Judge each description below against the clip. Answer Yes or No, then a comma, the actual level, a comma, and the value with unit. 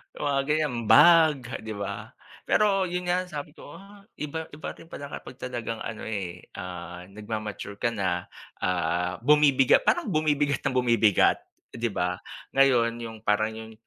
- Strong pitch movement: Yes, wide, 6.4 semitones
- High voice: No, low, 120 Hz